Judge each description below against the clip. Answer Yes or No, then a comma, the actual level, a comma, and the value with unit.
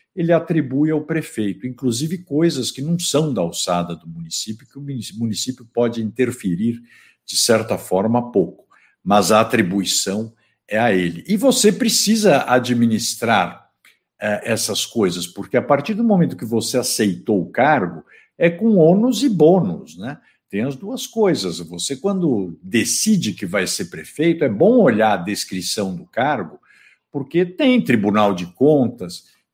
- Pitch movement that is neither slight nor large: No, wide, 8.2 semitones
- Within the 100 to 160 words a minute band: Yes, average, 150 wpm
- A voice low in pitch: Yes, low, 125 Hz